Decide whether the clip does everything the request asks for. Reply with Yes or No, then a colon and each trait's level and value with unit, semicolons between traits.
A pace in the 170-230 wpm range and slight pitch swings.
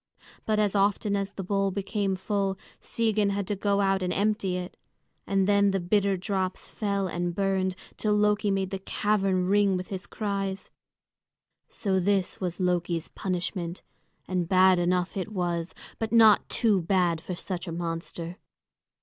No: average, 160 wpm; narrow, 1.9 semitones